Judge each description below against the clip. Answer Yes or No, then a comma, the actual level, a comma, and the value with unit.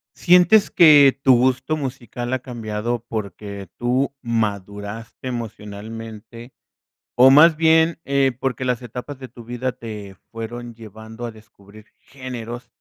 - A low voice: Yes, low, 120 Hz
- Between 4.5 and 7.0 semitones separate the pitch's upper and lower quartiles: No, average, 3.1 semitones